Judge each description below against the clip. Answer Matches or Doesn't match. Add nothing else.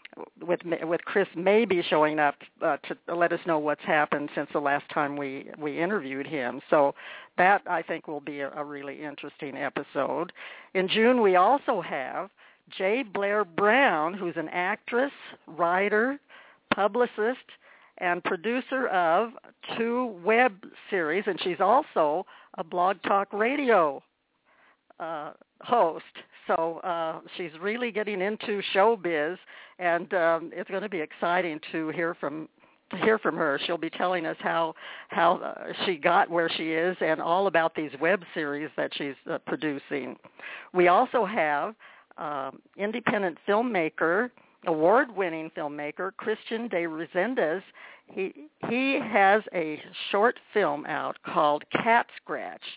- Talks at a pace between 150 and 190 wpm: Doesn't match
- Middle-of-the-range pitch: Matches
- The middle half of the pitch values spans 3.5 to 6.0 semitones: Matches